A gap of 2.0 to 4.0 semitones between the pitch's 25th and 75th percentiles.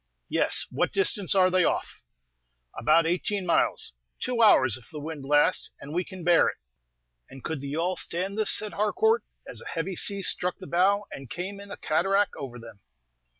No: average, 4.9 semitones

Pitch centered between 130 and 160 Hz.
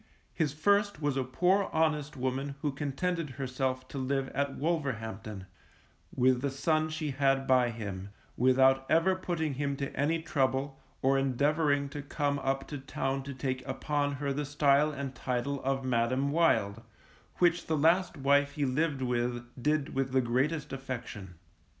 Yes: medium, 140 Hz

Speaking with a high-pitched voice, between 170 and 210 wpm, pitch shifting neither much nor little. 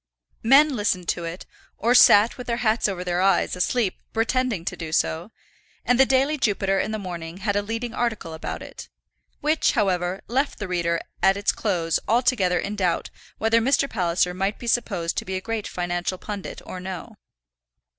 Yes: high, 200 Hz; average, 185 wpm; average, 4.6 semitones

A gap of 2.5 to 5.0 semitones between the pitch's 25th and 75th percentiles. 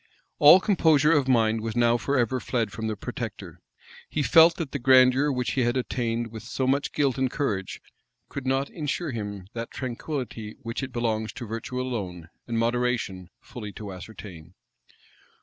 Yes: average, 3.4 semitones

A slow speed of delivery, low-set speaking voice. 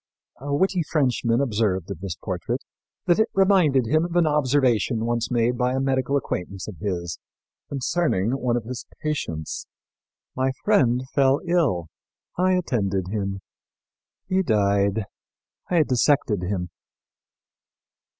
Yes: slow, 130 wpm; low, 125 Hz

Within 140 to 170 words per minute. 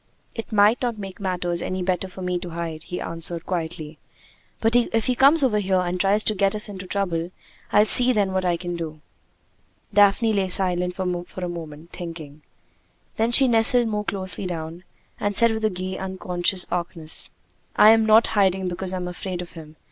No: average, 185 wpm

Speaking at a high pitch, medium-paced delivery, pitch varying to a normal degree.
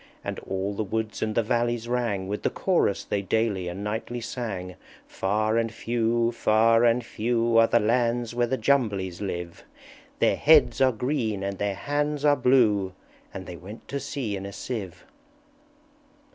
No: low, 115 Hz; average, 170 wpm; average, 3.2 semitones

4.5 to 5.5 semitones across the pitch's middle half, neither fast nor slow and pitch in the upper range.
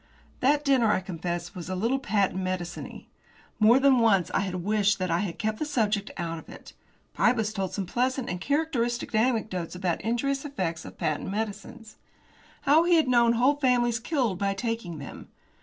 Yes: average, 5.2 semitones; average, 180 wpm; high, 215 Hz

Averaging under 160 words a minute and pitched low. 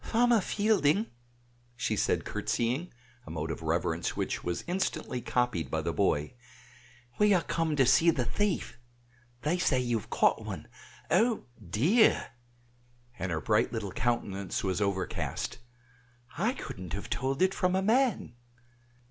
Yes: average, 145 wpm; low, 130 Hz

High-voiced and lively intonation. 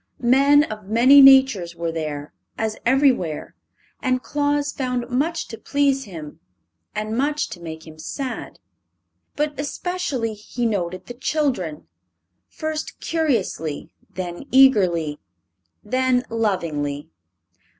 Yes: high, 240 Hz; wide, 8.2 semitones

